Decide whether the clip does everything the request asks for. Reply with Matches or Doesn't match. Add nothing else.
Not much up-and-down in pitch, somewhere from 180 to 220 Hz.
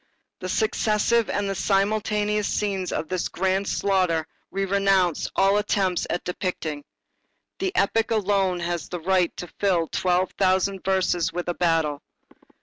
Matches